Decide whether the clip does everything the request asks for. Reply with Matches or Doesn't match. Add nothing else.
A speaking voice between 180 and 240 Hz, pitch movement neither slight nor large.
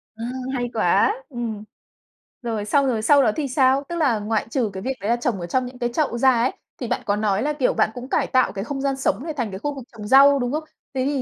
Doesn't match